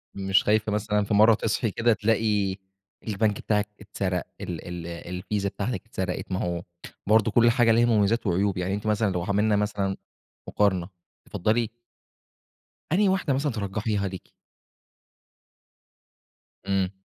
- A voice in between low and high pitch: No, low, 105 Hz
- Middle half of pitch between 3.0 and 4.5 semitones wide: No, narrow, 2.5 semitones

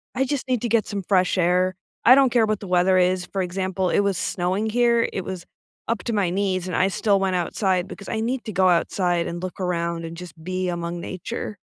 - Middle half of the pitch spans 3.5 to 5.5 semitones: No, average, 2.9 semitones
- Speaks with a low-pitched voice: No, medium, 185 Hz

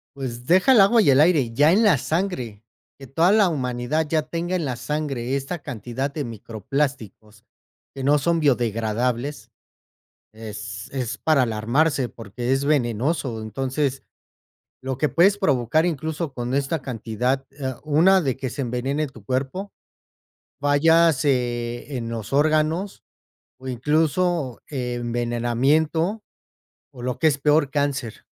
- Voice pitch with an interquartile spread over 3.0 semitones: Yes, average, 4.4 semitones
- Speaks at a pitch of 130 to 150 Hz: Yes, low, 135 Hz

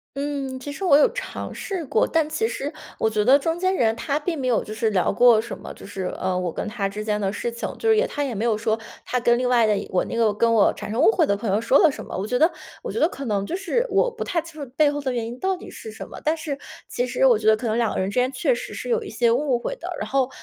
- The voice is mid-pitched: No, very high, 250 Hz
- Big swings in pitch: Yes, wide, 5.8 semitones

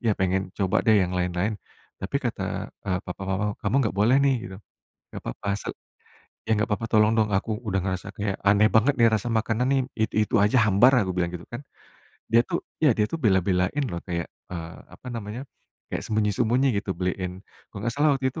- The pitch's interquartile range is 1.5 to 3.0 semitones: No, average, 3.6 semitones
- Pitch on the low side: Yes, low, 105 Hz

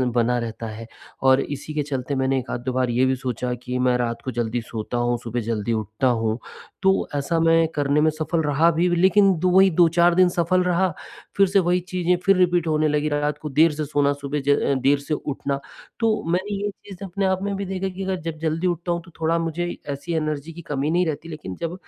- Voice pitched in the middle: Yes, medium, 155 Hz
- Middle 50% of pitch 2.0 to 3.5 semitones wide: No, average, 5.0 semitones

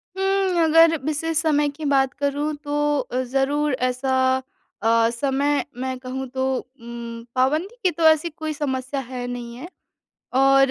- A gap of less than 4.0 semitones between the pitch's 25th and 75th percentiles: Yes, average, 3.1 semitones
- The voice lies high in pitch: Yes, very high, 280 Hz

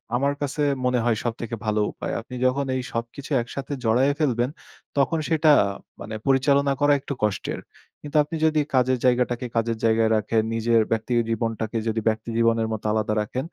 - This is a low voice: Yes, low, 120 Hz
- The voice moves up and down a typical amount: Yes, average, 3.6 semitones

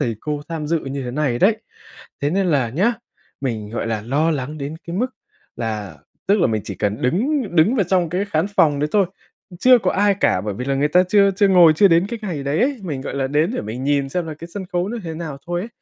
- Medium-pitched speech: Yes, medium, 160 Hz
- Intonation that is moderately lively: No, wide, 5.9 semitones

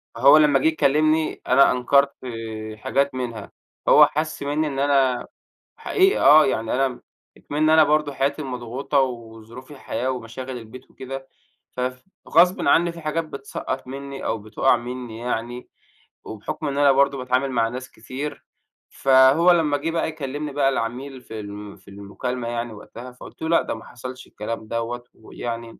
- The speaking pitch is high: No, low, 130 Hz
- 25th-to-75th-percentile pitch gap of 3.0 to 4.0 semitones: Yes, average, 3.4 semitones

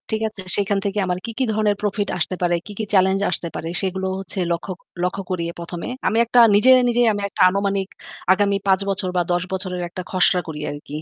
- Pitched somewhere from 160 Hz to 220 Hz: Yes, high, 190 Hz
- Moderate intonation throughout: No, narrow, 2.2 semitones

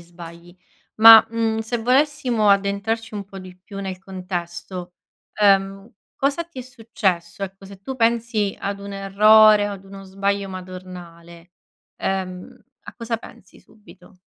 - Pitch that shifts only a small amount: No, average, 3.2 semitones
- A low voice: No, high, 200 Hz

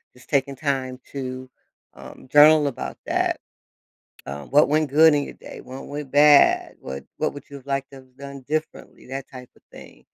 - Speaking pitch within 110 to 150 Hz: Yes, medium, 140 Hz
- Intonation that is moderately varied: No, narrow, 2.1 semitones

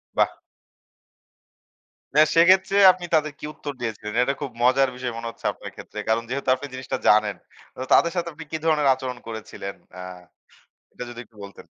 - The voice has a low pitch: Yes, low, 130 Hz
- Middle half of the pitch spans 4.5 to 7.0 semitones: Yes, average, 4.9 semitones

